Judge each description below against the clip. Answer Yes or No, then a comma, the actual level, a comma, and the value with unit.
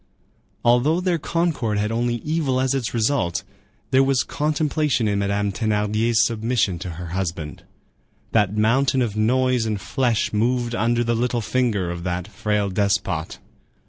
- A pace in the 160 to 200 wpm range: No, average, 150 wpm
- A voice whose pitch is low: Yes, low, 115 Hz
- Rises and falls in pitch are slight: No, average, 3.9 semitones